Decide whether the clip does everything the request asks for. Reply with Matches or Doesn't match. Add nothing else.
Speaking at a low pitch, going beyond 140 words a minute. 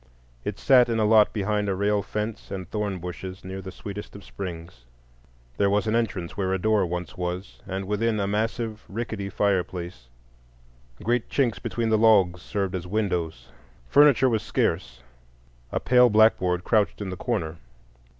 Matches